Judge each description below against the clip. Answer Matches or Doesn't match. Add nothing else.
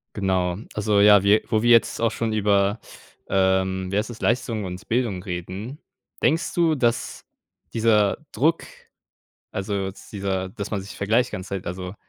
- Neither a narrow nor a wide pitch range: Matches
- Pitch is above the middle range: Doesn't match